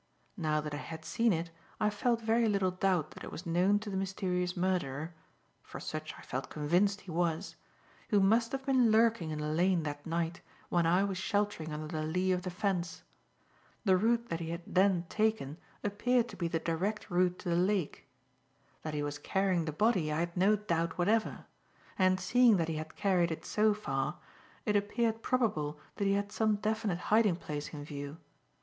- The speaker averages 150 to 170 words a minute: No, average, 195 wpm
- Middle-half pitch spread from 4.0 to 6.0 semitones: Yes, average, 4.3 semitones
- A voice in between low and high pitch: Yes, medium, 180 Hz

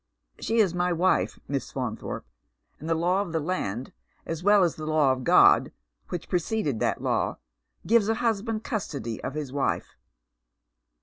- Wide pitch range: Yes, wide, 5.8 semitones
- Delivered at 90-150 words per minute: No, average, 170 wpm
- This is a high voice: No, medium, 170 Hz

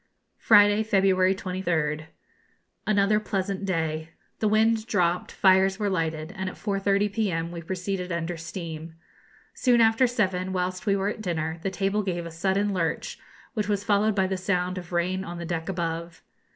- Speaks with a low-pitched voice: No, high, 190 Hz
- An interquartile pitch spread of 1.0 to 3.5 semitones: Yes, average, 3.0 semitones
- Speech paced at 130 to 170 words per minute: Yes, average, 165 wpm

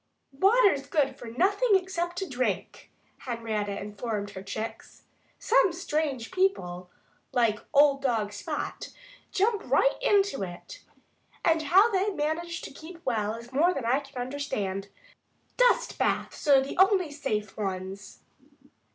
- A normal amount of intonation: No, wide, 9.0 semitones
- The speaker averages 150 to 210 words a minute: No, slow, 135 wpm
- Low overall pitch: No, very high, 275 Hz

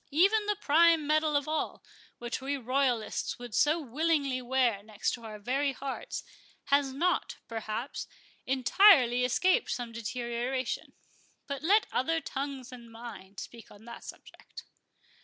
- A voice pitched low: No, very high, 265 Hz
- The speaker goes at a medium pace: No, slow, 130 wpm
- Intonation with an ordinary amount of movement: Yes, average, 4.3 semitones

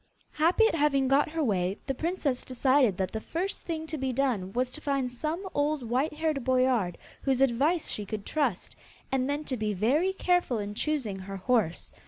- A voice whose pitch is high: Yes, very high, 265 Hz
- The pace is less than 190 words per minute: No, average, 195 wpm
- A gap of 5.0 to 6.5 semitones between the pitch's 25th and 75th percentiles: Yes, wide, 5.5 semitones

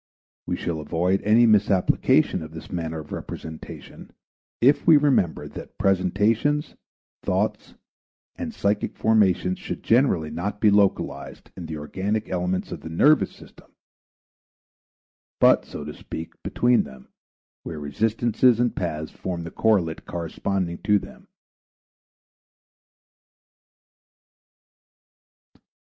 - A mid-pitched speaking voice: No, very low, 95 Hz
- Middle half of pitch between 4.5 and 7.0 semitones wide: Yes, average, 5.2 semitones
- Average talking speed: No, slow, 110 wpm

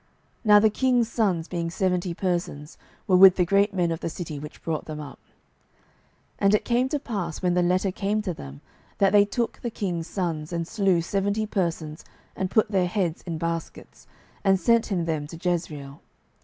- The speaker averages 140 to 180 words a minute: No, average, 195 wpm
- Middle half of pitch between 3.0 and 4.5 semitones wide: Yes, average, 3.5 semitones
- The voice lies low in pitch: No, medium, 180 Hz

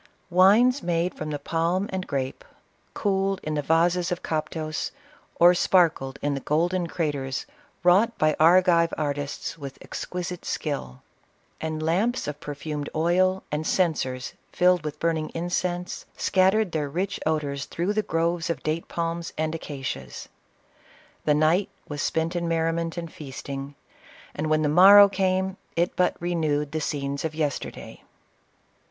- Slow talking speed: No, average, 150 wpm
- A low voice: No, medium, 165 Hz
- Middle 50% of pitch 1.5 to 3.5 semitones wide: Yes, average, 3.2 semitones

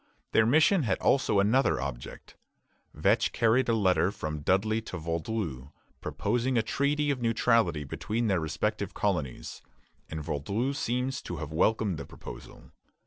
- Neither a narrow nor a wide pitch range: No, wide, 7.4 semitones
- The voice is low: Yes, low, 110 Hz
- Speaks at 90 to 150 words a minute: Yes, average, 140 wpm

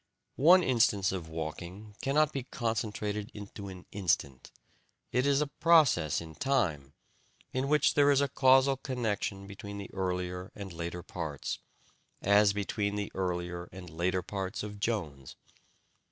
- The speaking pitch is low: Yes, low, 100 Hz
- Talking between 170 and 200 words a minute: No, average, 140 wpm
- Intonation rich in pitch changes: Yes, wide, 6.0 semitones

